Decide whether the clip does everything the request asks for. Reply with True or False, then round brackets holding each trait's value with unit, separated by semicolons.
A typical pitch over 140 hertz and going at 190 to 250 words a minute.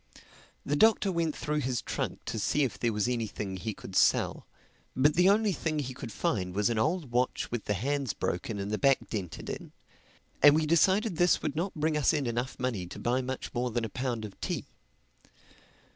False (130 Hz; 205 wpm)